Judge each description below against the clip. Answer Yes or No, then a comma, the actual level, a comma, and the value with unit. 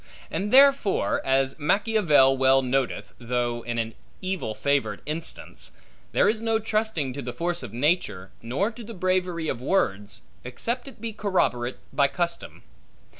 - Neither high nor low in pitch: Yes, medium, 150 Hz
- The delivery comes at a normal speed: Yes, average, 150 wpm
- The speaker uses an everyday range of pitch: No, wide, 8.4 semitones